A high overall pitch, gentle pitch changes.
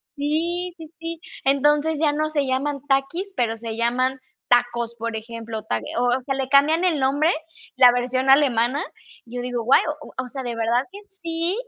No: very high, 265 Hz; average, 4.2 semitones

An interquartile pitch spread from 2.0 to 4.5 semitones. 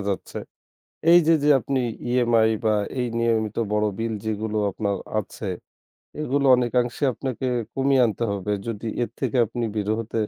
Yes: average, 2.9 semitones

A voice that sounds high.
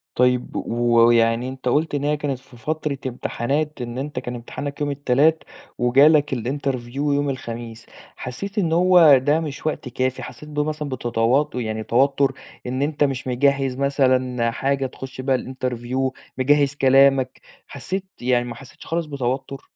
No: low, 135 Hz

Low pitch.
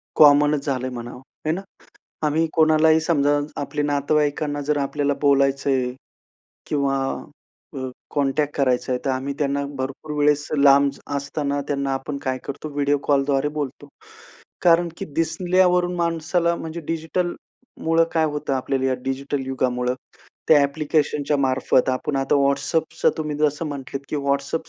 No: medium, 145 Hz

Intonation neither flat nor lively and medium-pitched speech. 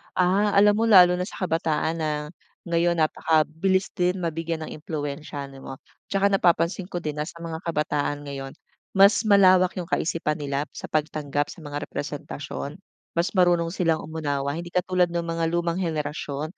Yes: average, 3.1 semitones; medium, 165 Hz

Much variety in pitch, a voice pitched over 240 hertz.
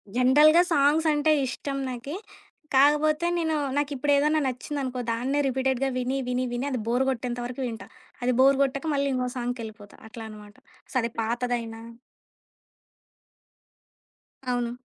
No: average, 2.8 semitones; very high, 260 Hz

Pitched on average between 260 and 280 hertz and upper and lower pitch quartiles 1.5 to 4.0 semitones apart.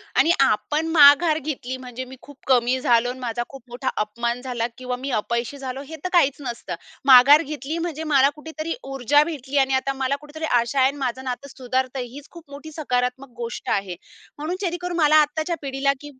Yes: very high, 270 Hz; average, 3.2 semitones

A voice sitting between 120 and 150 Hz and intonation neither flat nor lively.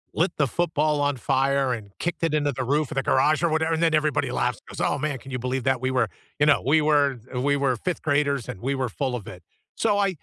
Yes: medium, 140 Hz; average, 3.0 semitones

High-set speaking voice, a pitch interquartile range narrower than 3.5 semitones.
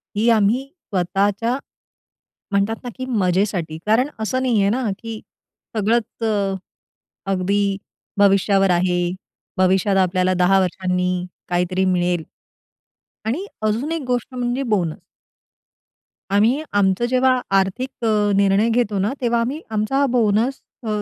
No: high, 205 Hz; average, 4.0 semitones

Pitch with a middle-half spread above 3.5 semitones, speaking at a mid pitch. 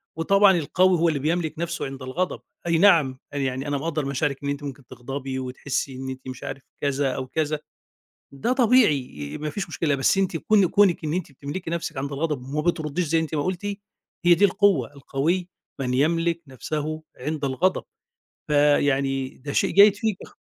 Yes: average, 4.1 semitones; medium, 150 Hz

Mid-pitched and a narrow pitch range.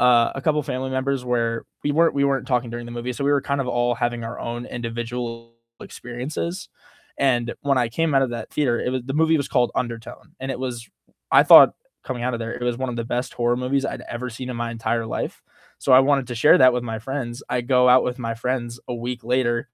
No: low, 125 Hz; narrow, 1.9 semitones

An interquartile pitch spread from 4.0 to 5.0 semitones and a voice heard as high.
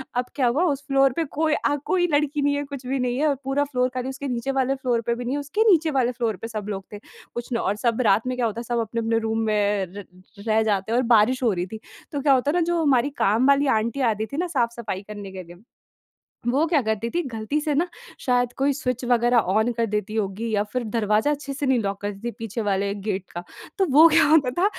Yes: average, 4.4 semitones; high, 245 Hz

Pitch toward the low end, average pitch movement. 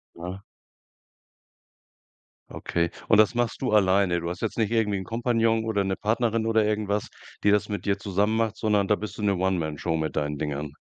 Yes: low, 105 Hz; average, 3.4 semitones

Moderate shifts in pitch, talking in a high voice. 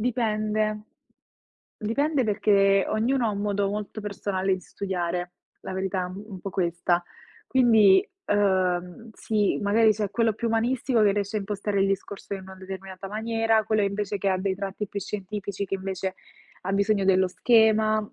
No: narrow, 2.2 semitones; high, 200 Hz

